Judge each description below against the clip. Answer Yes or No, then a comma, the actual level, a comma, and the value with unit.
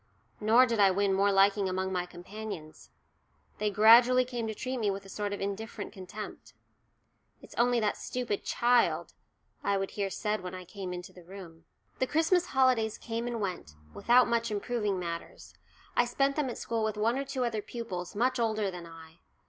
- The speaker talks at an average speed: Yes, average, 190 wpm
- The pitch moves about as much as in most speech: Yes, average, 3.9 semitones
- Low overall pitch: No, high, 210 Hz